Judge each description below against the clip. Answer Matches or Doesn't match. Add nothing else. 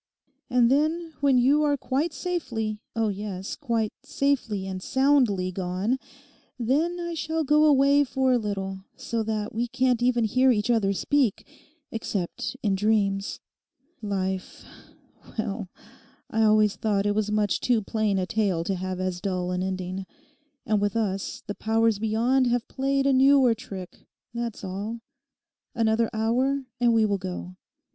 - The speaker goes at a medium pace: Matches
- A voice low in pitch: Doesn't match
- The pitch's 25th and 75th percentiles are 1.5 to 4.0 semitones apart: Doesn't match